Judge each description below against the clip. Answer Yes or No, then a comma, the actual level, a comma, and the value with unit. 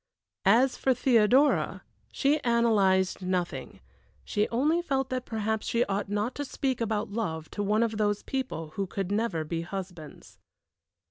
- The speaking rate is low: No, average, 150 wpm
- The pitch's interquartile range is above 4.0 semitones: Yes, average, 4.6 semitones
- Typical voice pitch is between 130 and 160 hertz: No, high, 215 Hz